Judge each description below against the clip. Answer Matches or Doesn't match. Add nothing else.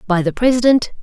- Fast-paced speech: Doesn't match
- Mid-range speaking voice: Doesn't match